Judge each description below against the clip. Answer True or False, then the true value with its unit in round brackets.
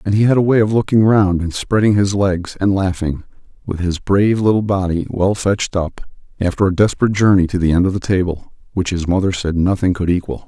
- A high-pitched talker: False (95 Hz)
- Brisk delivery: True (225 wpm)